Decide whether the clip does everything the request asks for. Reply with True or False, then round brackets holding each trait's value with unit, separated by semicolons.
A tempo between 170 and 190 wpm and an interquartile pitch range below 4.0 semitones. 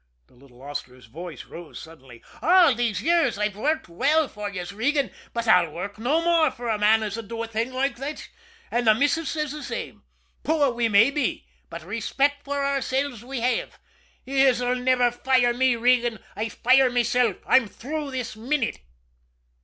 False (175 wpm; 4.7 semitones)